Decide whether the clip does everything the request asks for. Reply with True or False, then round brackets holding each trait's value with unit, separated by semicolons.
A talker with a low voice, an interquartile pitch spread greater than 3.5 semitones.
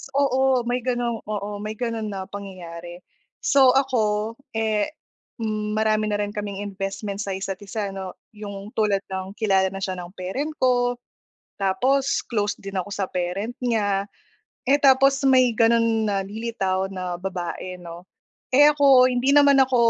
False (210 Hz; 4.1 semitones)